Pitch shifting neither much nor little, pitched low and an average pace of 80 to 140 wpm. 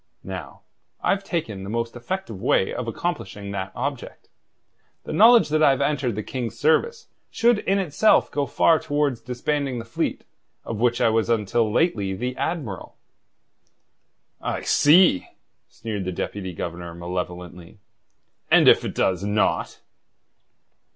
No: wide, 7.0 semitones; low, 120 Hz; slow, 135 wpm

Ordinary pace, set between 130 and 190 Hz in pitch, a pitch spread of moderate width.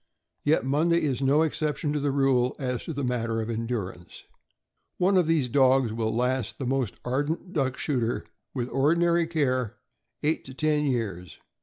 Yes: average, 165 wpm; low, 135 Hz; average, 3.7 semitones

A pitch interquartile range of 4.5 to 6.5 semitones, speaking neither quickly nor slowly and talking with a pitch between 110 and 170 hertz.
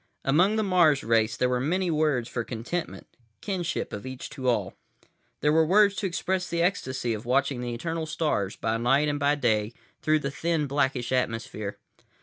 Yes: wide, 5.6 semitones; average, 180 wpm; medium, 140 Hz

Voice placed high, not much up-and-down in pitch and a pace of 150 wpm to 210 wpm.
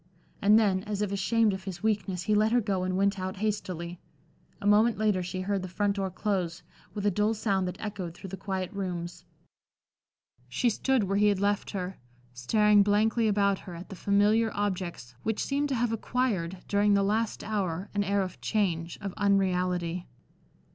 Yes: high, 200 Hz; narrow, 2.3 semitones; average, 190 wpm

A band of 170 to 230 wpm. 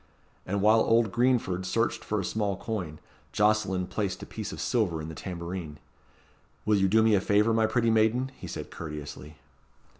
Yes: average, 180 wpm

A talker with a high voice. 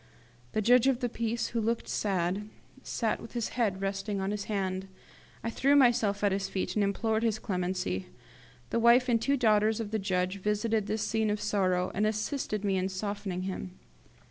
Yes: high, 210 Hz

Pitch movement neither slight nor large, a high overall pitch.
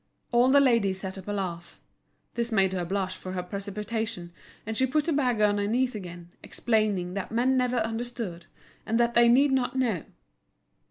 Yes: average, 4.3 semitones; high, 220 Hz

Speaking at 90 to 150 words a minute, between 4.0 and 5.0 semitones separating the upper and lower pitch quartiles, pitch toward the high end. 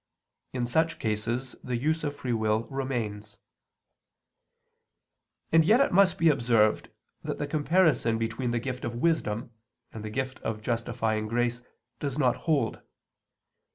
No: average, 140 wpm; average, 4.6 semitones; low, 120 Hz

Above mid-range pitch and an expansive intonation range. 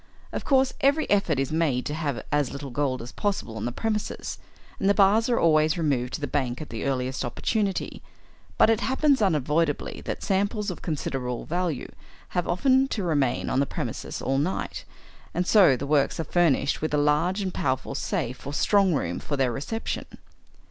No: medium, 155 Hz; wide, 6.5 semitones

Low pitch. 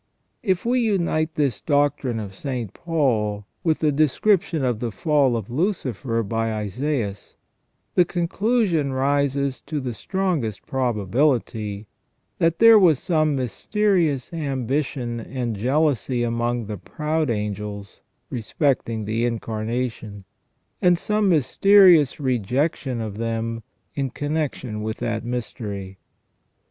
Yes: low, 130 Hz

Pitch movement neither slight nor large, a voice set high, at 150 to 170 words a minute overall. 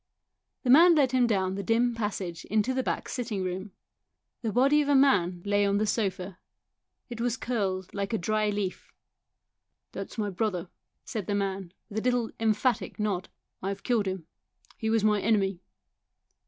No: average, 3.6 semitones; high, 210 Hz; average, 185 wpm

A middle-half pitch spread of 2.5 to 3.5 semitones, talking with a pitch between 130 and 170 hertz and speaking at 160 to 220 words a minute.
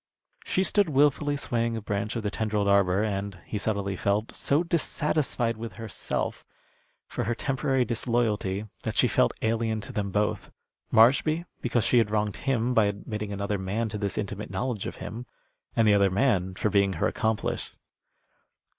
No: average, 3.1 semitones; low, 110 Hz; average, 170 wpm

